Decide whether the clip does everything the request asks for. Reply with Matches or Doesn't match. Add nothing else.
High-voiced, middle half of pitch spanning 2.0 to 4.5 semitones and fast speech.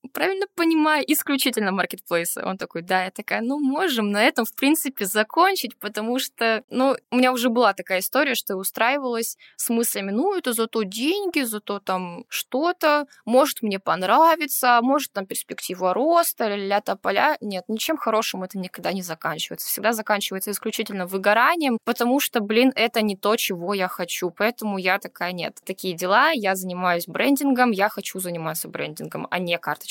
Doesn't match